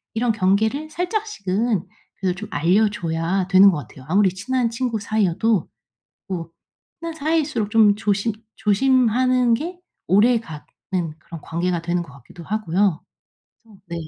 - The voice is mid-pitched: No, high, 205 Hz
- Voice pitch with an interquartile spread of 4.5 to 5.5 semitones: Yes, average, 5.1 semitones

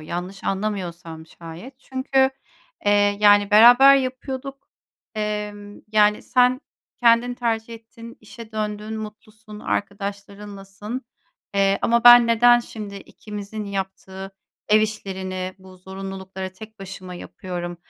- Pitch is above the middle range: Yes, high, 210 Hz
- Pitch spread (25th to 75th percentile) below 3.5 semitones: Yes, average, 3.1 semitones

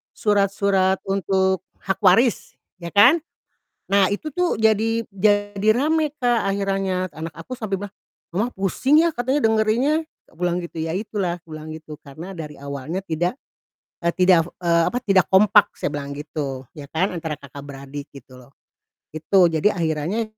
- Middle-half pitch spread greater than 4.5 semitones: Yes, average, 5.0 semitones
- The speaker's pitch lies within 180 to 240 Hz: Yes, high, 190 Hz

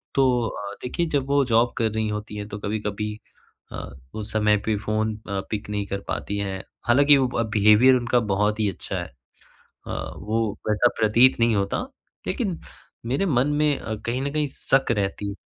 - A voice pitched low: Yes, low, 110 Hz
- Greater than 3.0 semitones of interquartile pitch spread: Yes, average, 3.5 semitones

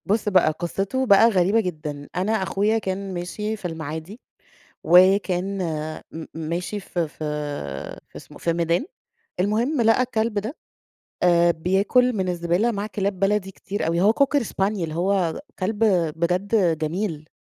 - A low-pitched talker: No, high, 190 Hz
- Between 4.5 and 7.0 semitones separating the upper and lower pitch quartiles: No, average, 3.7 semitones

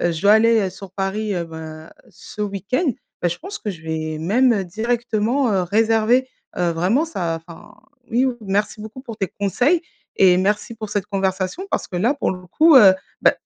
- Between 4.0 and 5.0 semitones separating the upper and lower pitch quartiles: Yes, average, 4.3 semitones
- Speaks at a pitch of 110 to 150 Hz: No, high, 205 Hz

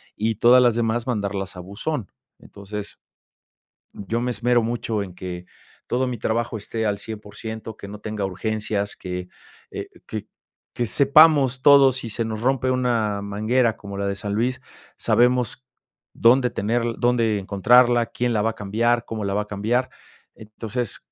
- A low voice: Yes, low, 110 Hz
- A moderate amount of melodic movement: Yes, average, 3.0 semitones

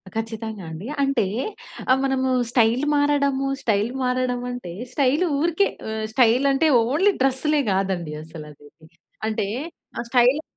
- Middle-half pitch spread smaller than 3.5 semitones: No, average, 4.2 semitones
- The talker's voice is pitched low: No, high, 245 Hz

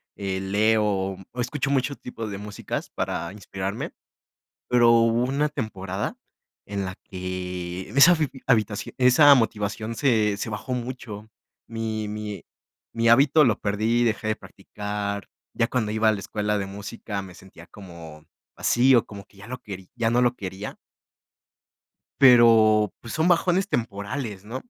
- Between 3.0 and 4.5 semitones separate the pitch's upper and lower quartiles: Yes, average, 3.4 semitones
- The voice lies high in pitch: No, low, 110 Hz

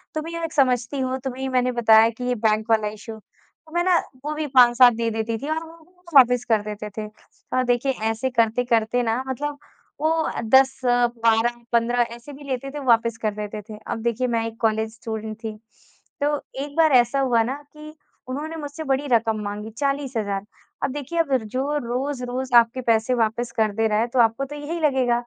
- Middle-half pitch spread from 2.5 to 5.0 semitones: Yes, average, 3.6 semitones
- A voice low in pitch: No, high, 245 Hz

